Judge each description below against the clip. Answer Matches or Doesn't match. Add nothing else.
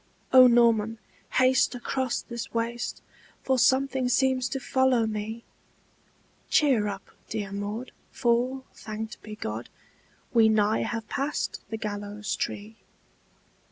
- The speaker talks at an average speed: Doesn't match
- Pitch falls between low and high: Doesn't match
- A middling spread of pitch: Matches